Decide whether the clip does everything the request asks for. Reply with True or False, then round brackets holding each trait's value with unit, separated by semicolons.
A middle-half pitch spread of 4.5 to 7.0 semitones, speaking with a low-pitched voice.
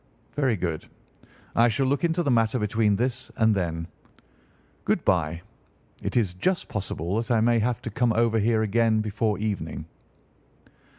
False (3.0 semitones; 110 Hz)